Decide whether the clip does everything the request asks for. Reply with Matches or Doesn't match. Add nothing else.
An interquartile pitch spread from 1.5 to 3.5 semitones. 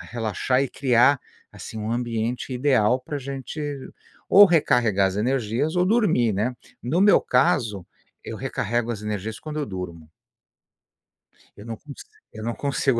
Doesn't match